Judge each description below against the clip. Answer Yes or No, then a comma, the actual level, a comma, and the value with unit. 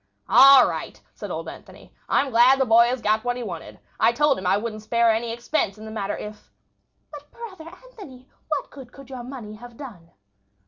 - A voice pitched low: No, high, 240 Hz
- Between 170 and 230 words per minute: Yes, average, 200 wpm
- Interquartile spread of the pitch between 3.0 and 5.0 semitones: Yes, average, 3.9 semitones